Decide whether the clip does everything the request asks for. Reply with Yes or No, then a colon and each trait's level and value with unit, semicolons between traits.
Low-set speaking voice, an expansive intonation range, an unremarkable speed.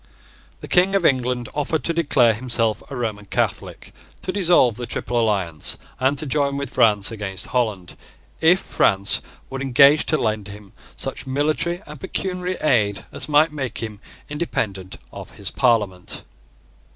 Yes: low, 125 Hz; wide, 6.0 semitones; average, 150 wpm